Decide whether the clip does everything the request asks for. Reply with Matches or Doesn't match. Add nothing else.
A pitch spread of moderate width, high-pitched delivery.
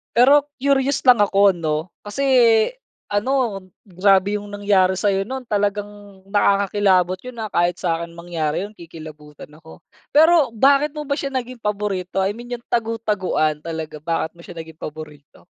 Doesn't match